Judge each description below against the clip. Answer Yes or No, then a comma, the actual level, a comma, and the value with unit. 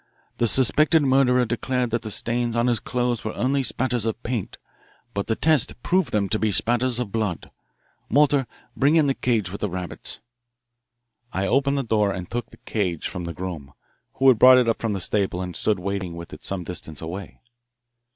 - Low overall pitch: Yes, low, 115 Hz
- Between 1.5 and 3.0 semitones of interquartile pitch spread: No, average, 4.6 semitones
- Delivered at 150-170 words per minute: No, average, 195 wpm